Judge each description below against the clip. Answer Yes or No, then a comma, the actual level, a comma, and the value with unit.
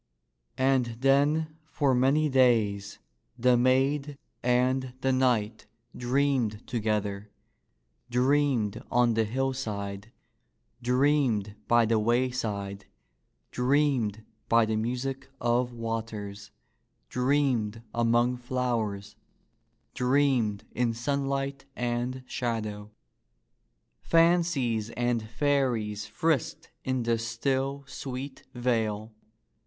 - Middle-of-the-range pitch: No, low, 120 Hz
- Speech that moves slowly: Yes, slow, 90 wpm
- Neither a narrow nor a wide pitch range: Yes, average, 3.2 semitones